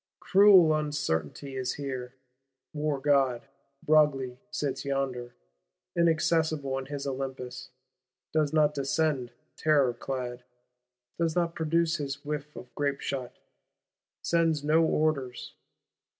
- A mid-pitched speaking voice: Yes, medium, 145 Hz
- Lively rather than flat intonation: No, average, 3.0 semitones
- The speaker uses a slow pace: Yes, slow, 105 wpm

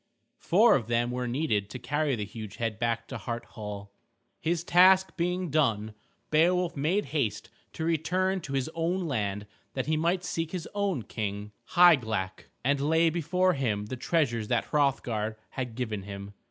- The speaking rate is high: No, average, 165 wpm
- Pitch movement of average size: No, wide, 7.3 semitones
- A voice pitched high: No, low, 135 Hz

